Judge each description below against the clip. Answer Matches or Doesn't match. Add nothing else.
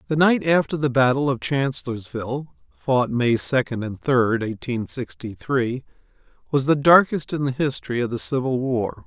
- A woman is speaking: Doesn't match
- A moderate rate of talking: Matches